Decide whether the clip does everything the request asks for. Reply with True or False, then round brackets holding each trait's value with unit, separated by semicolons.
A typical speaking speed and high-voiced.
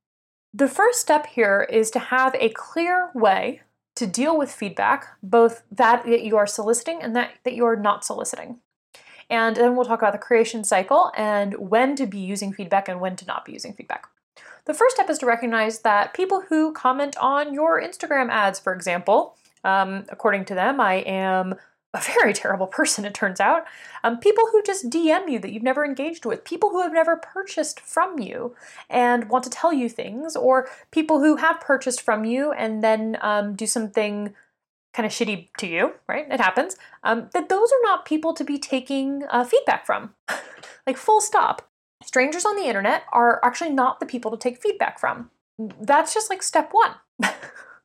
True (190 wpm; 250 Hz)